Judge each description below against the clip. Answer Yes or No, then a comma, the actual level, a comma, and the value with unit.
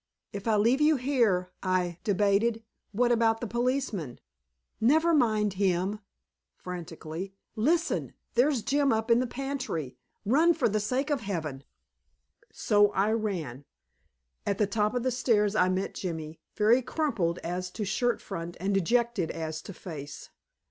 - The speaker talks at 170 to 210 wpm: No, average, 150 wpm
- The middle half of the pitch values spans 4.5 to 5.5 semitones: Yes, average, 5.1 semitones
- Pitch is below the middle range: No, high, 210 Hz